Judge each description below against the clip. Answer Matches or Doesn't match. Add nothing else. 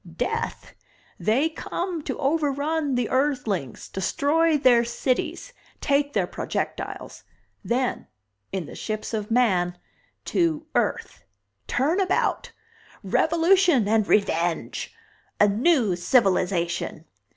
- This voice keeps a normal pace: Doesn't match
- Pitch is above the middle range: Matches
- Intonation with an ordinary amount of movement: Doesn't match